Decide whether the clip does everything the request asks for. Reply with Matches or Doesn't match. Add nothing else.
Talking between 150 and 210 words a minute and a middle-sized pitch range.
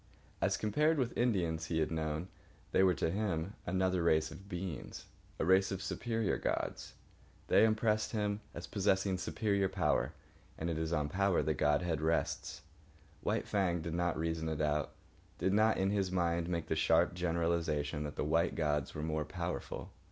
Matches